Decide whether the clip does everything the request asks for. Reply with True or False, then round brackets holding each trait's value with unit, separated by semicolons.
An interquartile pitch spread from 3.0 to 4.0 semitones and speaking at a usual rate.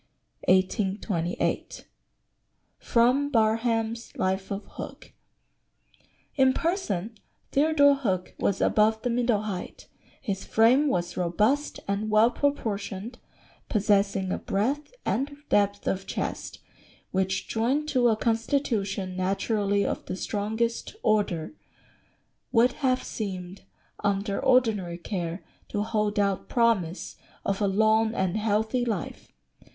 False (3.4 semitones; 110 wpm)